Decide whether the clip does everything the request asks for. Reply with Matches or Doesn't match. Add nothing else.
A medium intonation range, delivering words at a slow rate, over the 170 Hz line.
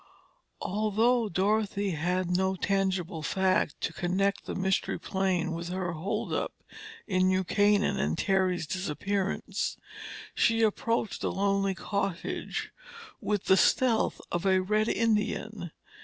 Doesn't match